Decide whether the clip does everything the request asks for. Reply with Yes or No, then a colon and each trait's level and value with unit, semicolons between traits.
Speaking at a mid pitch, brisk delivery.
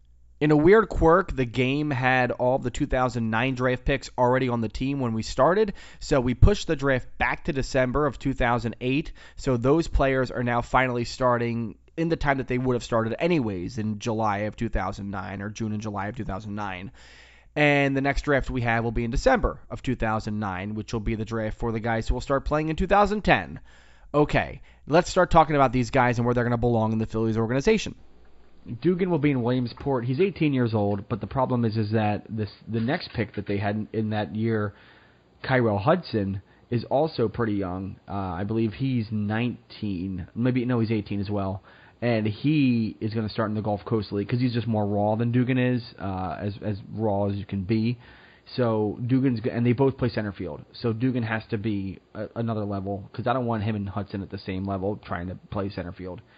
No: low, 115 Hz; fast, 215 wpm